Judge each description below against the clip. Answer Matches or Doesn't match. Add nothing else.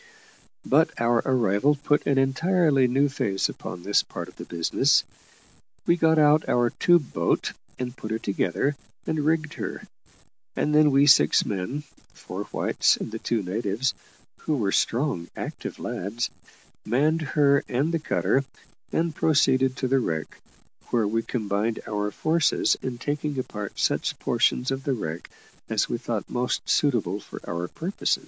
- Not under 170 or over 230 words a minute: Doesn't match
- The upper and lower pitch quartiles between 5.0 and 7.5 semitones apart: Matches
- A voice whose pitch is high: Doesn't match